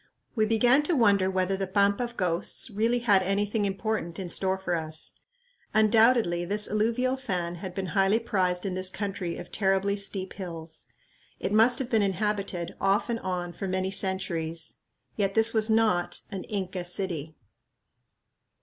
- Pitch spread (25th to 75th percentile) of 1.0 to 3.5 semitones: Yes, average, 3.1 semitones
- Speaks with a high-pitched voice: Yes, high, 195 Hz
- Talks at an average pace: Yes, average, 160 wpm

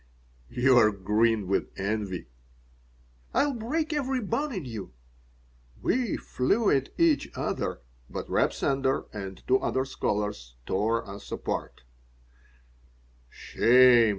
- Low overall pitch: Yes, low, 125 Hz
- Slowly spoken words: Yes, slow, 110 wpm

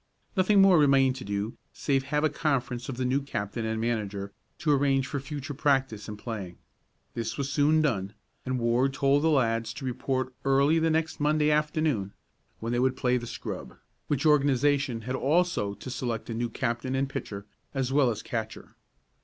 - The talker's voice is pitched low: Yes, low, 130 Hz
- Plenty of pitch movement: No, average, 3.7 semitones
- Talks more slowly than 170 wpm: No, average, 185 wpm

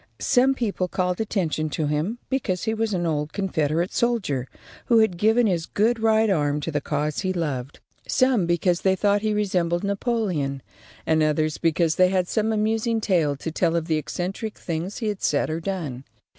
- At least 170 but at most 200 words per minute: Yes, average, 185 wpm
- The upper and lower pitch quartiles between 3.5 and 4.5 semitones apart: No, wide, 5.5 semitones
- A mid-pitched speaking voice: Yes, medium, 180 Hz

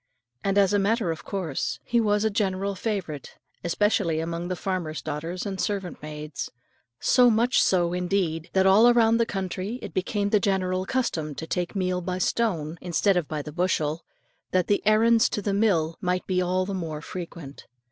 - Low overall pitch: No, medium, 185 Hz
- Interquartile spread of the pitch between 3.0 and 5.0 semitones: Yes, average, 3.5 semitones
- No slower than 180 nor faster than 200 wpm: Yes, average, 190 wpm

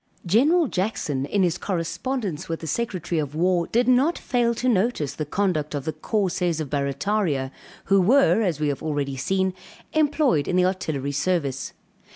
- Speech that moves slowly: No, average, 170 wpm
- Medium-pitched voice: Yes, medium, 180 Hz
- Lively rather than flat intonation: Yes, wide, 6.8 semitones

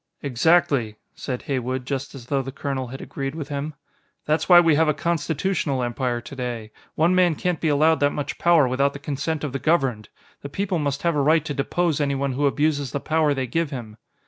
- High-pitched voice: No, medium, 140 Hz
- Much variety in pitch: No, average, 3.2 semitones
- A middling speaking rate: No, fast, 210 wpm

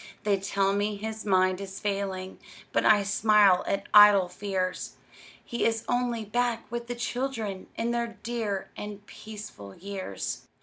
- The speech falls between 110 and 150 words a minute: Yes, average, 145 wpm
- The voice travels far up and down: No, average, 2.7 semitones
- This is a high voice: Yes, high, 205 Hz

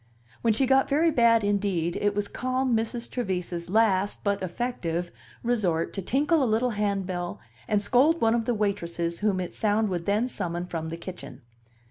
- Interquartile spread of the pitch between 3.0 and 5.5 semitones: Yes, average, 4.9 semitones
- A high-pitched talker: Yes, high, 205 Hz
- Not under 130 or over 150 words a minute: No, average, 175 wpm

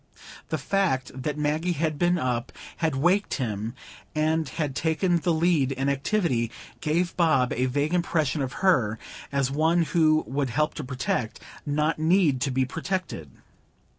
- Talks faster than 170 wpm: No, average, 155 wpm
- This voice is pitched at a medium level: Yes, medium, 150 Hz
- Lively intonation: No, average, 4.2 semitones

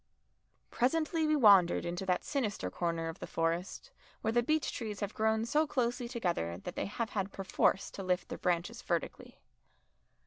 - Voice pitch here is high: Yes, high, 205 Hz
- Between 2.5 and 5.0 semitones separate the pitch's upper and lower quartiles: No, wide, 5.4 semitones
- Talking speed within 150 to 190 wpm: Yes, average, 170 wpm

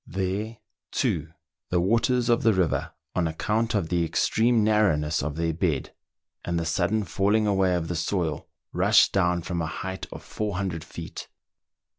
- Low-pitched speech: Yes, very low, 90 Hz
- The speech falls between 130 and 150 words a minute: No, average, 160 wpm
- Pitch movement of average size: Yes, average, 4.2 semitones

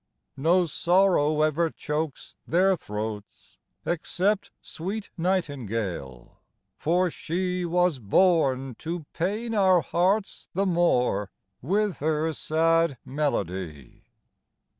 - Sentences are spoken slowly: Yes, slow, 95 wpm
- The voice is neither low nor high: Yes, medium, 165 Hz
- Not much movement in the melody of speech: No, average, 5.2 semitones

